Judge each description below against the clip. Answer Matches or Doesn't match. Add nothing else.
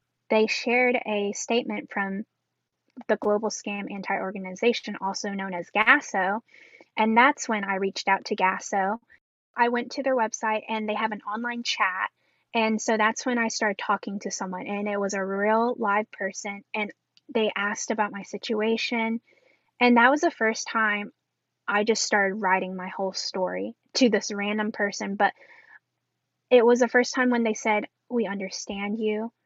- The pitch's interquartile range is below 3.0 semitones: Matches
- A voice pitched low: Doesn't match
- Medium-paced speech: Matches